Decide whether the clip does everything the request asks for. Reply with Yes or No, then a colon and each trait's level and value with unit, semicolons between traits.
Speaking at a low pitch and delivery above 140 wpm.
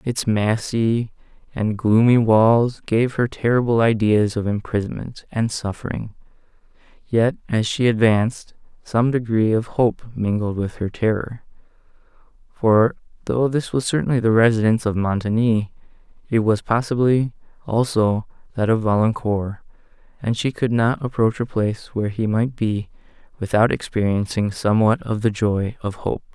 No: low, 110 Hz; slow, 135 wpm